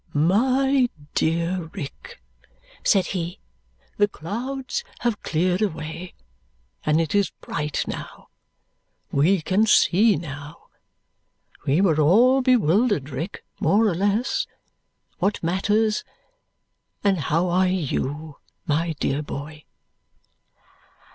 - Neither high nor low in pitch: Yes, medium, 180 Hz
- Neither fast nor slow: No, slow, 100 wpm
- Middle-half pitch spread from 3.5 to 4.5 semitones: No, average, 5.2 semitones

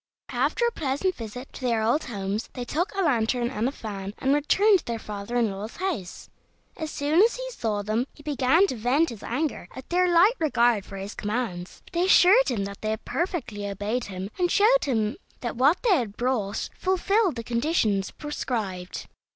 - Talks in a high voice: Yes, high, 245 Hz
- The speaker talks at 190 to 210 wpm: Yes, average, 200 wpm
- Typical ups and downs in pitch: No, wide, 7.8 semitones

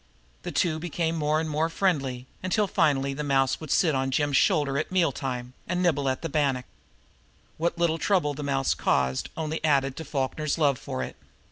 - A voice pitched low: No, medium, 150 Hz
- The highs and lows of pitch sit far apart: No, average, 3.3 semitones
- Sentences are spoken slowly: No, average, 190 wpm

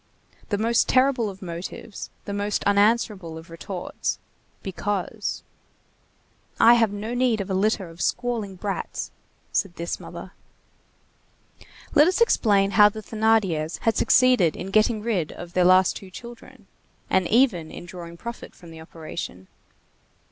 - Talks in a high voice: Yes, high, 200 Hz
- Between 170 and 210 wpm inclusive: No, average, 140 wpm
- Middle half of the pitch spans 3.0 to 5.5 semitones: Yes, average, 4.3 semitones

